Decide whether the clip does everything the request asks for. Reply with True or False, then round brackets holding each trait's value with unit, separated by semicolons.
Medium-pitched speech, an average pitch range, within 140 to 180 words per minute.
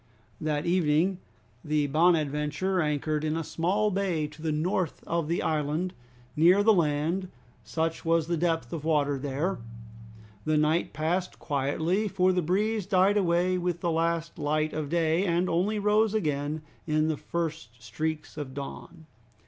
True (165 Hz; 3.0 semitones; 155 wpm)